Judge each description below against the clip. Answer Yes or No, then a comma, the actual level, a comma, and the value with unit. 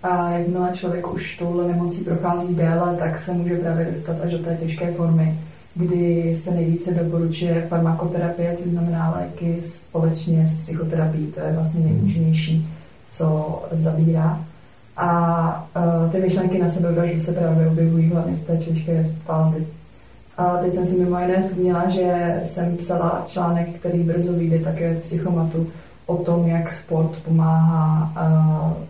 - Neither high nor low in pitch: Yes, medium, 170 Hz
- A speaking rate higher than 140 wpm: Yes, average, 150 wpm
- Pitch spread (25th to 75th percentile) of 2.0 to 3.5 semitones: No, narrow, 1.2 semitones